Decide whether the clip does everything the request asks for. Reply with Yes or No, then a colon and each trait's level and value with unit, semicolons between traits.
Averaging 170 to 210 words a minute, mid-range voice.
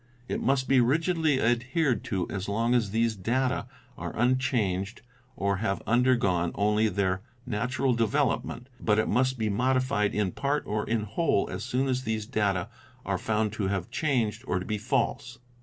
No: average, 175 wpm; low, 115 Hz